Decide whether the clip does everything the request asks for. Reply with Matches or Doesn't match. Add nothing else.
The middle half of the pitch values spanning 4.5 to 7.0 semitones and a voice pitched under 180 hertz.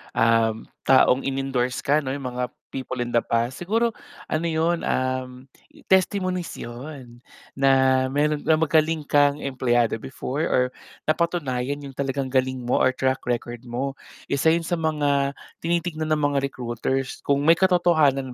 Doesn't match